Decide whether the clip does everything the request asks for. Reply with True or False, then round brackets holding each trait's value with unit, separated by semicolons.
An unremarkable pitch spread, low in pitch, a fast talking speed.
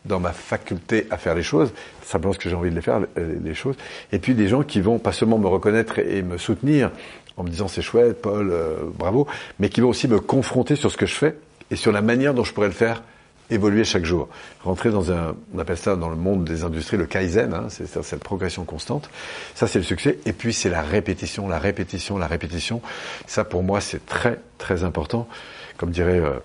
True (4.3 semitones; 100 Hz; 235 wpm)